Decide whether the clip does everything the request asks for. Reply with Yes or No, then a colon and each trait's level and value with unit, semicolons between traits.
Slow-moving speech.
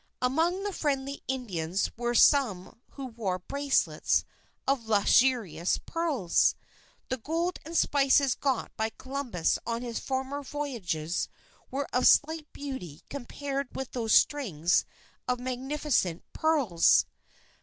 Yes: slow, 115 wpm